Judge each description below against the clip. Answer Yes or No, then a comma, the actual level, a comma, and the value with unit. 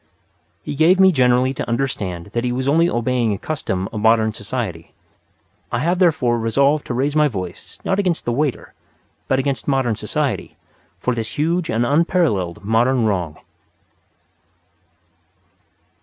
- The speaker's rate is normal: Yes, average, 145 wpm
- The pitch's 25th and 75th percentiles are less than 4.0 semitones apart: No, average, 5.0 semitones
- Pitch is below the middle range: Yes, low, 125 Hz